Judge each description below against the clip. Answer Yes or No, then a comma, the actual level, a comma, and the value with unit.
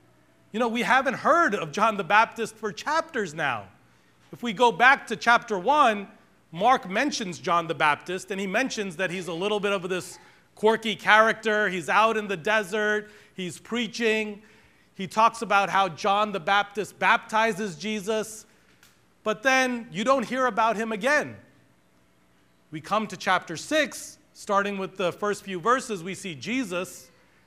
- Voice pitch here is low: No, high, 210 Hz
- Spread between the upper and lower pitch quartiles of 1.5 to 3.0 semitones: No, average, 3.5 semitones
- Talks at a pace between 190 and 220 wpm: No, average, 160 wpm